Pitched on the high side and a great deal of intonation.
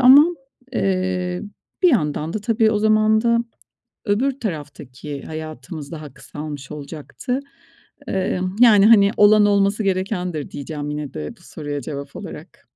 No: medium, 180 Hz; wide, 6.4 semitones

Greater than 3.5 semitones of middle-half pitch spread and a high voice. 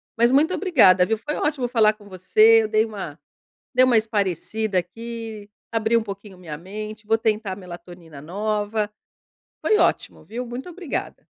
No: average, 3.1 semitones; high, 215 Hz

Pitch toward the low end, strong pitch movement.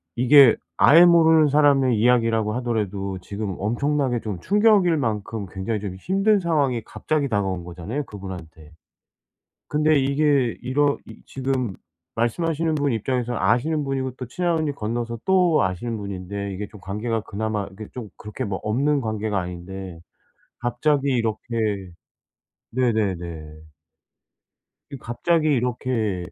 Yes: low, 120 Hz; wide, 5.9 semitones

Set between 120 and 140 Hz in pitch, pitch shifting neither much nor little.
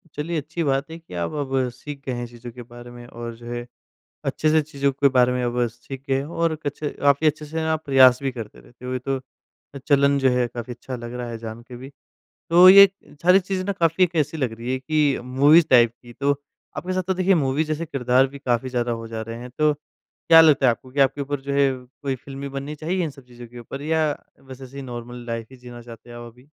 Yes: low, 135 Hz; average, 3.8 semitones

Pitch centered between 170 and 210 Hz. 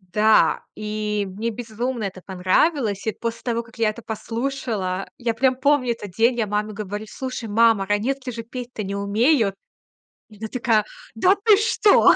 No: high, 225 Hz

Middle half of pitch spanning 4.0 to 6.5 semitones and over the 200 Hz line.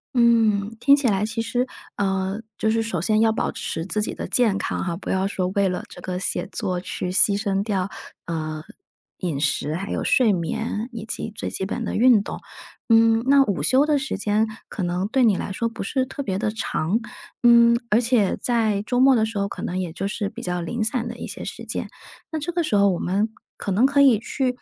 No: average, 3.6 semitones; high, 215 Hz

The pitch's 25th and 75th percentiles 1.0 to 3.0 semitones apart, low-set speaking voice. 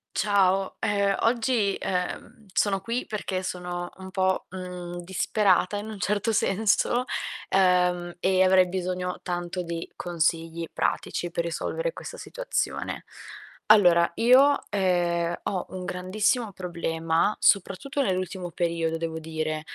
No: narrow, 2.6 semitones; medium, 185 Hz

